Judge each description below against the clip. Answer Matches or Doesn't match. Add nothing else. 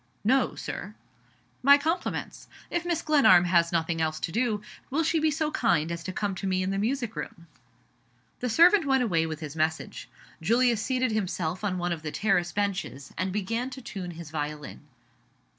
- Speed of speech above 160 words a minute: Matches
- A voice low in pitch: Doesn't match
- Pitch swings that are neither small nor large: Doesn't match